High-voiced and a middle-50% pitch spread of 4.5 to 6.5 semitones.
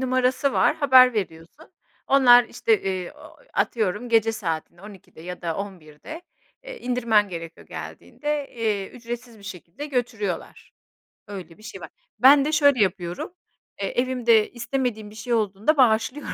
Yes: high, 225 Hz; average, 4.9 semitones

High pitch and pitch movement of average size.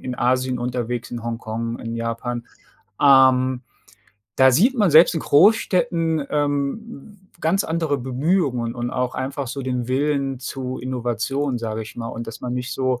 No: low, 130 Hz; average, 3.1 semitones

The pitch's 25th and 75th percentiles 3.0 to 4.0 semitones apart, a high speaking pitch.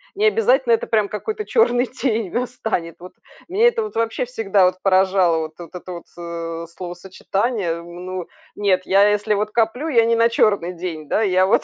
No: average, 4.7 semitones; high, 205 Hz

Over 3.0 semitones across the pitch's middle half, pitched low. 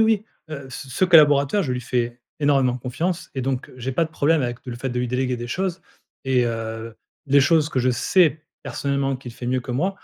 Yes: average, 3.7 semitones; low, 130 Hz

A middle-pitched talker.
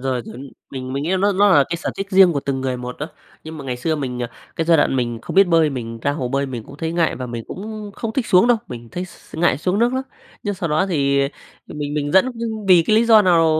Yes: medium, 155 Hz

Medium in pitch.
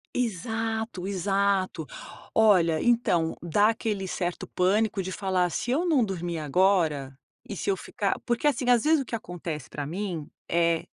No: high, 195 Hz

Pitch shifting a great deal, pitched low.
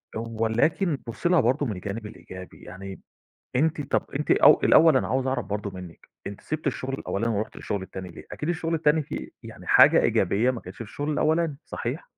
Yes: wide, 7.0 semitones; low, 130 Hz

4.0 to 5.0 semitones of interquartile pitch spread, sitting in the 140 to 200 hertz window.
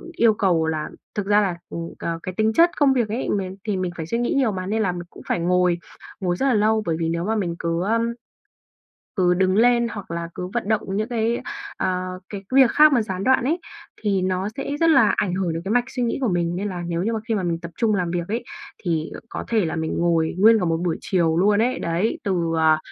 Yes: average, 4.4 semitones; high, 190 Hz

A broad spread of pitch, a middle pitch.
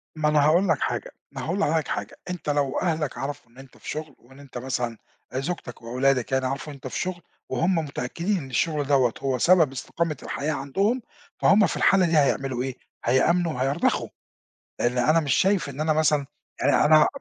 No: average, 3.8 semitones; medium, 145 Hz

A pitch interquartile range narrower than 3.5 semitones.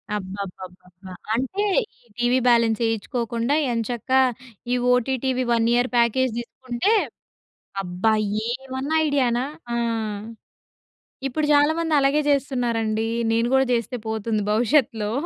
Yes: average, 2.9 semitones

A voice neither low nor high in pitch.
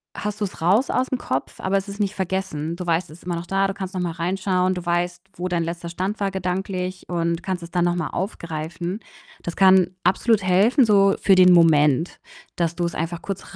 Yes: medium, 180 Hz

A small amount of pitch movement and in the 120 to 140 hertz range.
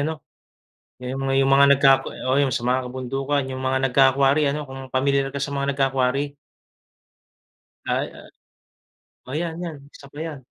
Yes: narrow, 1.2 semitones; low, 135 Hz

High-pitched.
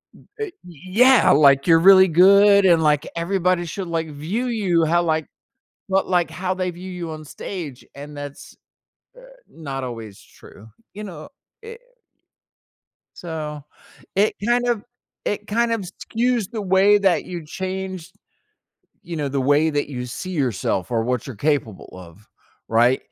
No: medium, 170 Hz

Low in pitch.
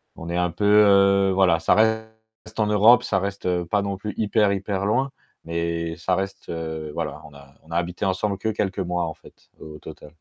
Yes: very low, 95 Hz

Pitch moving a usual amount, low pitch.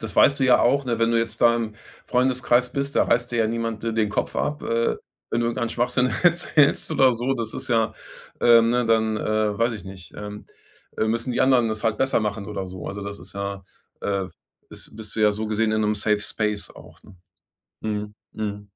No: narrow, 2.3 semitones; low, 115 Hz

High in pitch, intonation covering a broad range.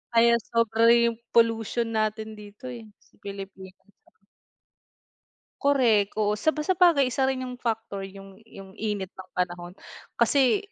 No: high, 220 Hz; average, 3.9 semitones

